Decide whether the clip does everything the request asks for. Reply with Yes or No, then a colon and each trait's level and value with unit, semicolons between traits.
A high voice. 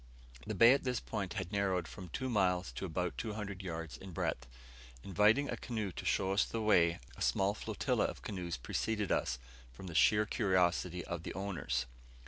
No: very low, 95 Hz